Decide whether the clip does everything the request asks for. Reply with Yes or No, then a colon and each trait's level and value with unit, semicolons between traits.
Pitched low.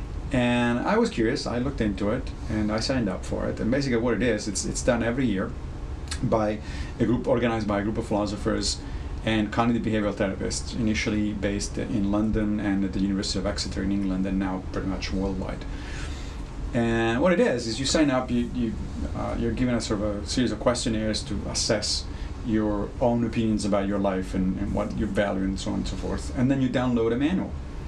Yes: low, 105 Hz